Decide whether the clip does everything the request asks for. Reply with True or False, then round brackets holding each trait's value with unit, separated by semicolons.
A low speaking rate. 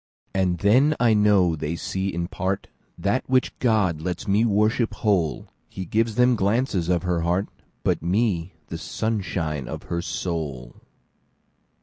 True (130 wpm)